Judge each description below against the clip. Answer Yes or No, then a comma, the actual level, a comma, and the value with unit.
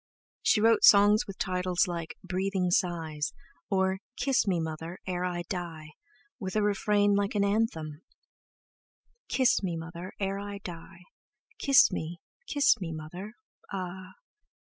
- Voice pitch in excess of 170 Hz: Yes, medium, 185 Hz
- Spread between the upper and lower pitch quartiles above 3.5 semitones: No, average, 2.9 semitones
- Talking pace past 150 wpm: No, slow, 135 wpm